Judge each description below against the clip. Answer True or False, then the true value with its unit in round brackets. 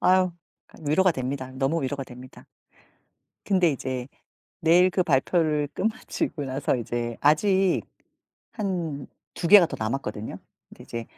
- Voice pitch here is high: False (145 Hz)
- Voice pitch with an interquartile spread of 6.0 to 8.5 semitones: False (5.6 semitones)